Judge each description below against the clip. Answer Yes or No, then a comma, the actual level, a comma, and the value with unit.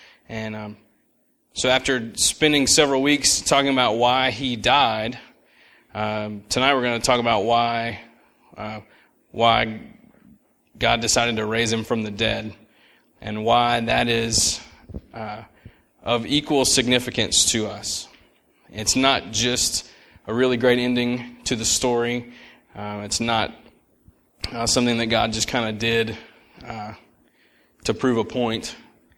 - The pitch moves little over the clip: Yes, narrow, 2.2 semitones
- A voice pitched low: Yes, low, 115 Hz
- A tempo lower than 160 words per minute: Yes, slow, 135 wpm